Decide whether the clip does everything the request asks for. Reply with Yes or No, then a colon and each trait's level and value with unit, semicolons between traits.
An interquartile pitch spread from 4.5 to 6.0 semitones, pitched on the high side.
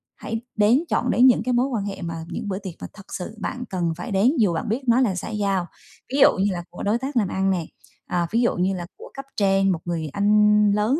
No: average, 3.8 semitones; high, 205 Hz